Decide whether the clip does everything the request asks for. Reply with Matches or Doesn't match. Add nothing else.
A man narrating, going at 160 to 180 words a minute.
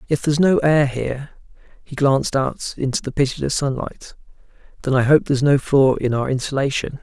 Matches